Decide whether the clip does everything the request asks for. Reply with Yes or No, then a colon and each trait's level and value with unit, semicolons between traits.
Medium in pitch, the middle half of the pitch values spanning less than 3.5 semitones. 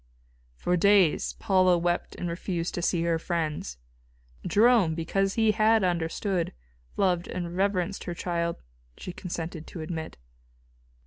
Yes: medium, 175 Hz; narrow, 2.5 semitones